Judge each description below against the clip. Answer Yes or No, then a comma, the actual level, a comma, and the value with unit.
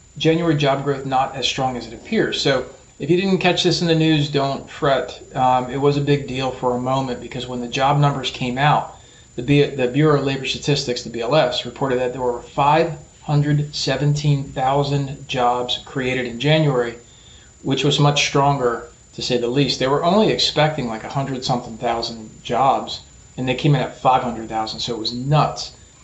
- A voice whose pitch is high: No, low, 135 Hz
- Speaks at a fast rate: No, average, 185 wpm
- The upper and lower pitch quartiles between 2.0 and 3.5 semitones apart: Yes, average, 2.8 semitones